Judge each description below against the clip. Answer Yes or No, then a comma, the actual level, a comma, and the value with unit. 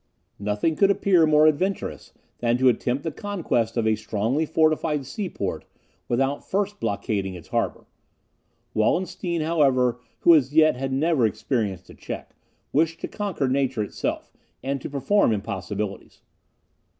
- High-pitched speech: No, low, 135 Hz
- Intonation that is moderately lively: No, wide, 6.4 semitones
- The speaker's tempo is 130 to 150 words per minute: Yes, average, 140 wpm